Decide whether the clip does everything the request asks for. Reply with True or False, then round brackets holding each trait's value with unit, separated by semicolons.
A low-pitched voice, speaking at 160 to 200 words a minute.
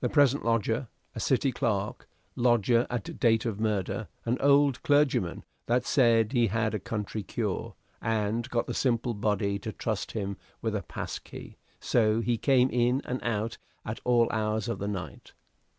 True (115 Hz; 165 wpm)